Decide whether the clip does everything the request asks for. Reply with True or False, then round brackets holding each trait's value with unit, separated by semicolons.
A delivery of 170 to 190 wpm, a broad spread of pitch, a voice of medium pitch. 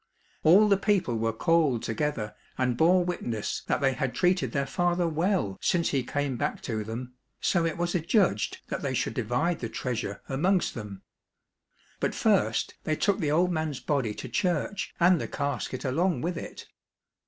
True (175 wpm; 6.1 semitones; 150 Hz)